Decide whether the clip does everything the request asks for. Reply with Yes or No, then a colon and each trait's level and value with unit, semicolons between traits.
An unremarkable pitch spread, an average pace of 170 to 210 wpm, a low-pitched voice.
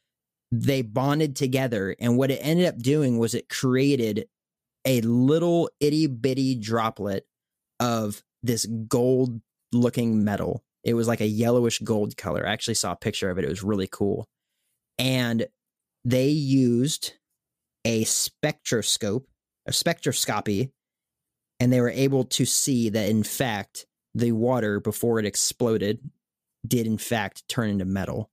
No: average, 3.2 semitones; average, 140 wpm; low, 120 Hz